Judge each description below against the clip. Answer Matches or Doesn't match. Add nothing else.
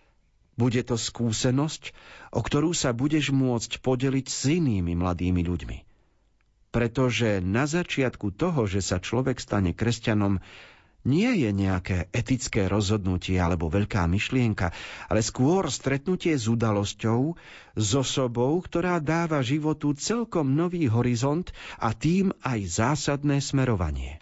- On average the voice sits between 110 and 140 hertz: Matches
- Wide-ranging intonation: Matches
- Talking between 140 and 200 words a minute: Doesn't match